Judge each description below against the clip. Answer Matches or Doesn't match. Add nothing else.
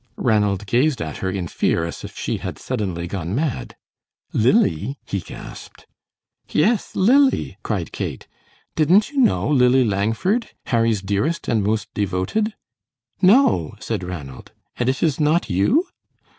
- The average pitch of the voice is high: Doesn't match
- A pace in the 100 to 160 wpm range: Matches